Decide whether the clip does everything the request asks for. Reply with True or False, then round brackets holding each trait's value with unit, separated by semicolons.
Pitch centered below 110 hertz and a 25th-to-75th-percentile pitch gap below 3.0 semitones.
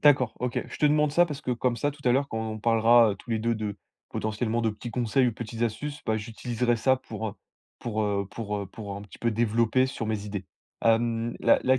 False (115 Hz; 2.6 semitones)